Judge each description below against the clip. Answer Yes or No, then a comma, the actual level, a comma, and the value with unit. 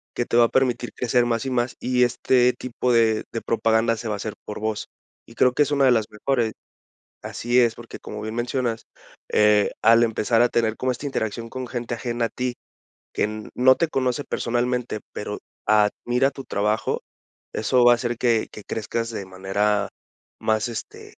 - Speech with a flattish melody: Yes, narrow, 2.2 semitones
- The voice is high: No, low, 115 Hz